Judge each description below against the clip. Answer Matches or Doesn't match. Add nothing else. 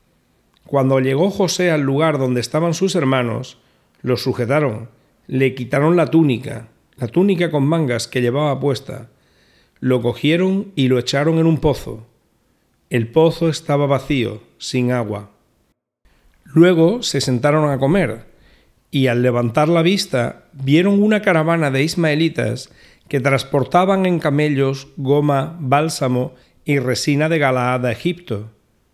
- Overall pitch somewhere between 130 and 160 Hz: Matches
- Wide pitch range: Doesn't match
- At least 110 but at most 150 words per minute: Matches